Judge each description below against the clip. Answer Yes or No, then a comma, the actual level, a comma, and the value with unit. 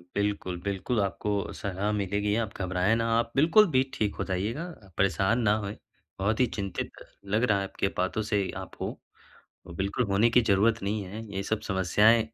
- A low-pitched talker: Yes, low, 100 Hz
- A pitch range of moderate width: No, narrow, 2.3 semitones